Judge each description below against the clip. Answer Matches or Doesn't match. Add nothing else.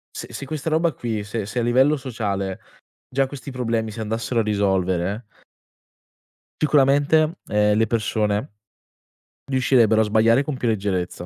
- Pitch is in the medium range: Doesn't match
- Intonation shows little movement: Doesn't match